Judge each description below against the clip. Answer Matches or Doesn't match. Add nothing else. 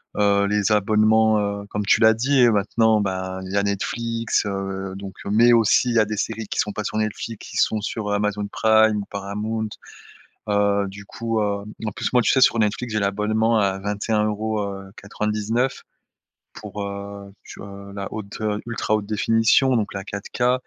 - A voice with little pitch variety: Matches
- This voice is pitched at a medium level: Doesn't match